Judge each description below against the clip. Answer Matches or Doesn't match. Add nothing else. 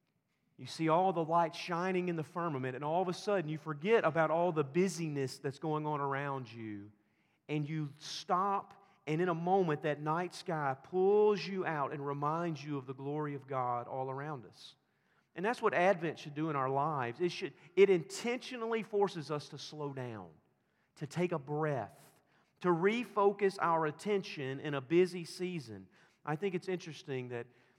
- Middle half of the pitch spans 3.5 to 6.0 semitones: Matches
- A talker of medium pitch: Matches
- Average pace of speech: Matches